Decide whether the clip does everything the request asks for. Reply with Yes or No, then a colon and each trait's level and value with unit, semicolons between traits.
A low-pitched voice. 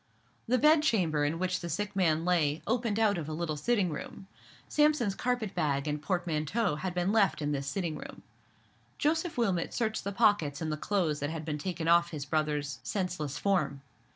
No: medium, 175 Hz